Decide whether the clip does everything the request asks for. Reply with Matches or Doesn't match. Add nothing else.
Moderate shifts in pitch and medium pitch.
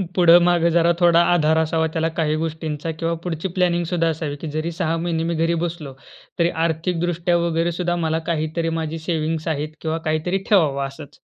Doesn't match